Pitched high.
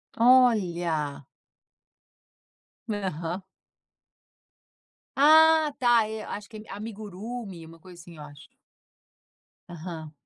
Yes: high, 195 Hz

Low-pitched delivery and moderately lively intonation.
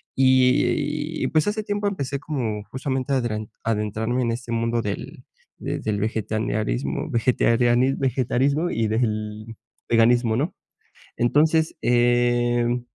Yes: low, 120 Hz; average, 3.1 semitones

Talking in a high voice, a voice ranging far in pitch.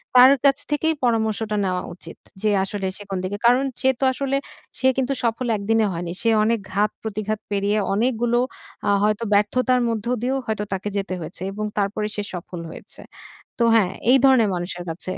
No: high, 215 Hz; average, 3.6 semitones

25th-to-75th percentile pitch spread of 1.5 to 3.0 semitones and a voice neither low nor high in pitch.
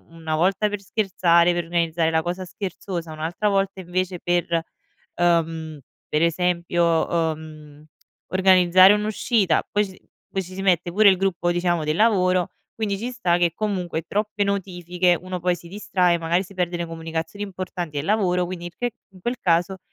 Yes: narrow, 2.4 semitones; medium, 180 Hz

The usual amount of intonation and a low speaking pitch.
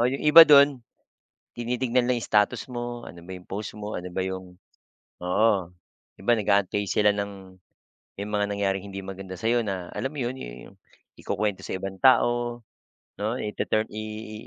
Yes: average, 3.7 semitones; low, 105 Hz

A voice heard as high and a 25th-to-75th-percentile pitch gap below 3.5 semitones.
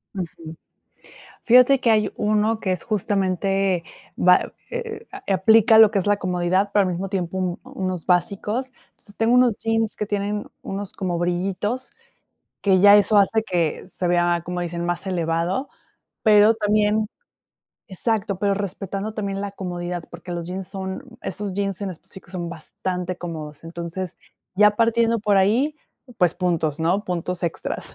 Yes: high, 195 Hz; average, 3.0 semitones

